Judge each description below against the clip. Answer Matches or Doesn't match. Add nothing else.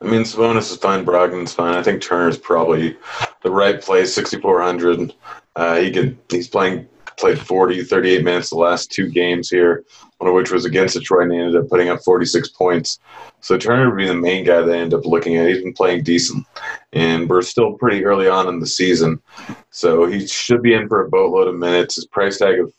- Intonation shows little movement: Matches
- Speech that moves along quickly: Matches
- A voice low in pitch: Matches